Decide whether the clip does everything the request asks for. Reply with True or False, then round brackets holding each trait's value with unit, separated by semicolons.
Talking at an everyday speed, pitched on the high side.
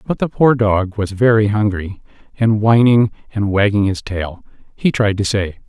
False (180 wpm; 105 Hz)